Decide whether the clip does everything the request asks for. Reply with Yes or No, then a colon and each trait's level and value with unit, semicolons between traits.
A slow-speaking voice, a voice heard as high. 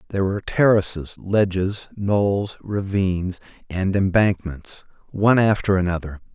No: slow, 105 wpm; very low, 95 Hz